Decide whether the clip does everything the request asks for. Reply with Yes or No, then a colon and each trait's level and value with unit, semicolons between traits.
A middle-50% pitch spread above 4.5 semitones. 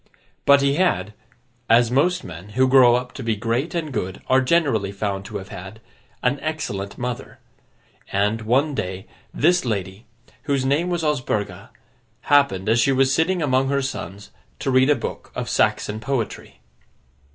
Yes: average, 5.1 semitones